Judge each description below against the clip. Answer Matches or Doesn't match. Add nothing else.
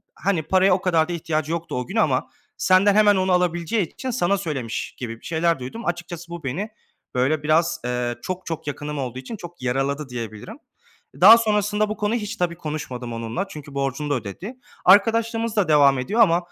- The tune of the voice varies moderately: Doesn't match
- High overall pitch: Doesn't match